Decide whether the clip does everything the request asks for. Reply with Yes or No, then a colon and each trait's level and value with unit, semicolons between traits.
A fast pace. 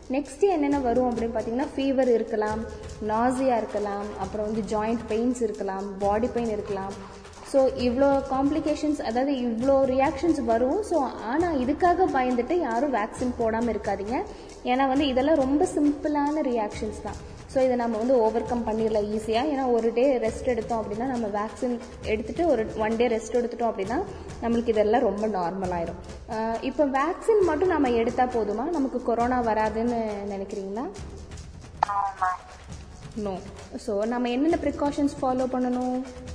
Yes: fast, 135 wpm